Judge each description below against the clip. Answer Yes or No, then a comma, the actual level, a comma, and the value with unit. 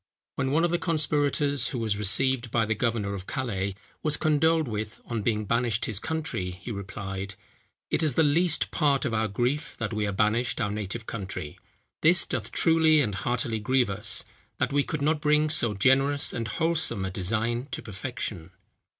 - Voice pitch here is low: Yes, low, 120 Hz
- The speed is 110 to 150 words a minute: No, average, 185 wpm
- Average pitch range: No, wide, 5.9 semitones